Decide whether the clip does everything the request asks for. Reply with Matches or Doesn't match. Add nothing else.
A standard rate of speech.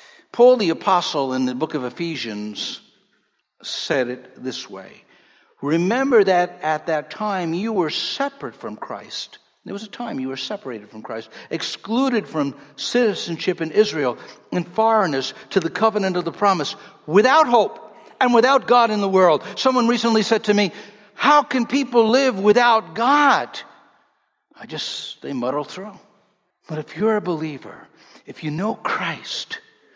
Matches